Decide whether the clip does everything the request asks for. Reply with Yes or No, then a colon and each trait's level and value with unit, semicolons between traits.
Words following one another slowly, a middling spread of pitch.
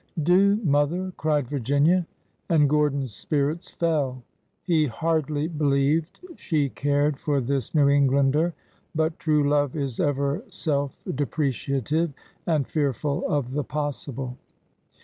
No: slow, 130 wpm; narrow, 2.2 semitones